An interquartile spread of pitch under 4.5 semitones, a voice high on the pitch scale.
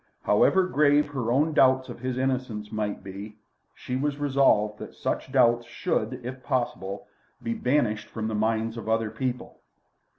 No: average, 3.4 semitones; low, 120 Hz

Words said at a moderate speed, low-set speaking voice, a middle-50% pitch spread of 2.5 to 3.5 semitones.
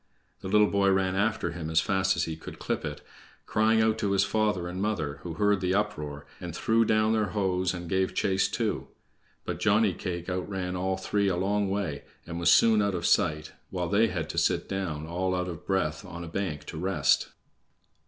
No: fast, 210 wpm; very low, 95 Hz; average, 2.8 semitones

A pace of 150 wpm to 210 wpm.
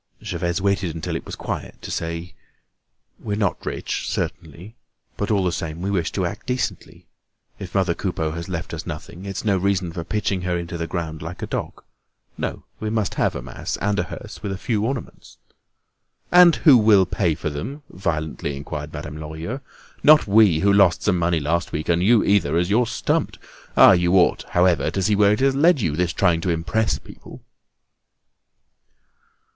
Yes: average, 190 wpm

